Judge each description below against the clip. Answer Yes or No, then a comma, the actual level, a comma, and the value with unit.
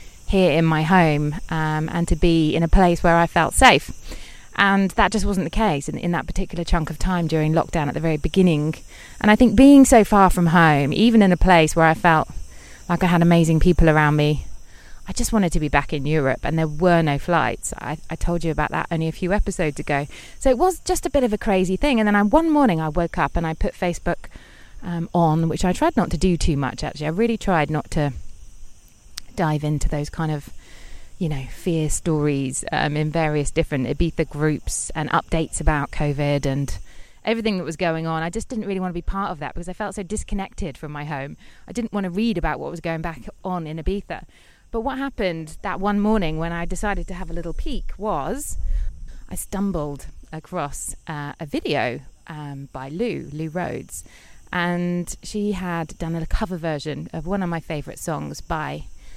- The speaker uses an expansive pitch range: No, average, 3.7 semitones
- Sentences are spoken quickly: Yes, fast, 215 wpm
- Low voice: No, medium, 165 Hz